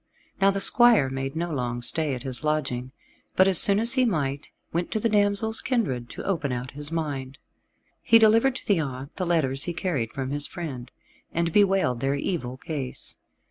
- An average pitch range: No, wide, 6.7 semitones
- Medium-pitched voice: Yes, medium, 155 Hz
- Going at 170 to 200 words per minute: Yes, average, 190 wpm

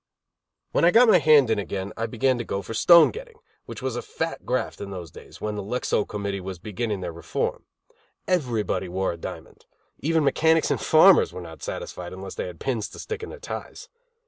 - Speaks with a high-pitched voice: No, low, 115 Hz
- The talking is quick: Yes, fast, 210 wpm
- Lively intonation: Yes, wide, 8.9 semitones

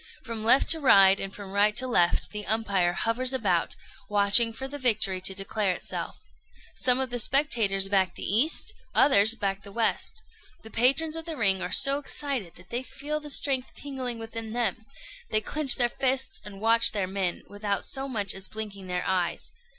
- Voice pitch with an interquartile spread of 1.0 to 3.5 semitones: No, average, 4.8 semitones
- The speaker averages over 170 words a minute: Yes, average, 190 wpm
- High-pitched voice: Yes, high, 220 Hz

